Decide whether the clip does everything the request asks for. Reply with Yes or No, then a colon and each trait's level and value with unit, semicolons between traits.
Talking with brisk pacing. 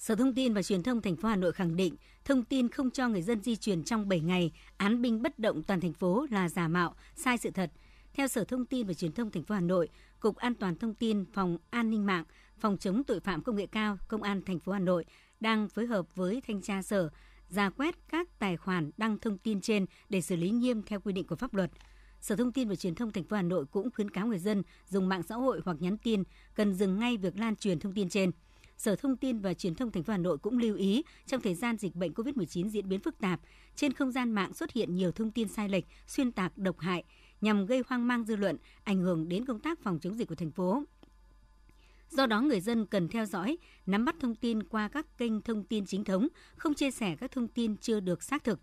Yes: fast, 260 wpm